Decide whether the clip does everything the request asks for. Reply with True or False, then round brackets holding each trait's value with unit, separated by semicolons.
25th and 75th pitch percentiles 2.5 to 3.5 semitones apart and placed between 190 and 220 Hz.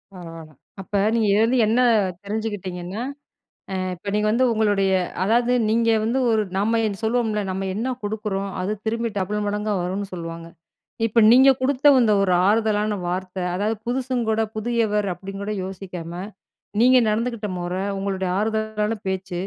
True (2.8 semitones; 210 Hz)